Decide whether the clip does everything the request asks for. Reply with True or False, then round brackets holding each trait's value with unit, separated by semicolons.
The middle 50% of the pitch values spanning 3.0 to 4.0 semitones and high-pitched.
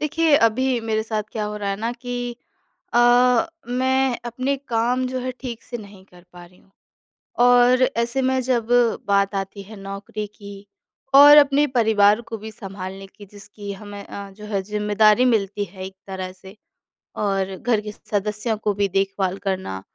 True (3.6 semitones; 210 Hz)